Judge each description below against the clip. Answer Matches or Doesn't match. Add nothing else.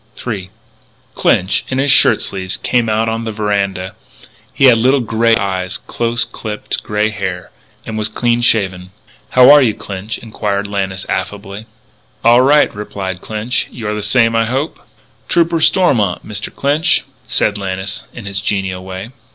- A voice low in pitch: Matches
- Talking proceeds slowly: Doesn't match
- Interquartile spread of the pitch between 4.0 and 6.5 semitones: Doesn't match